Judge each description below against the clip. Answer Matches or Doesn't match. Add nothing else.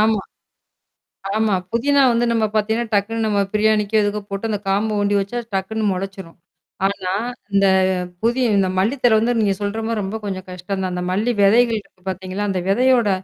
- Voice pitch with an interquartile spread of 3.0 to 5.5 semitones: Doesn't match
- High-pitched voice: Matches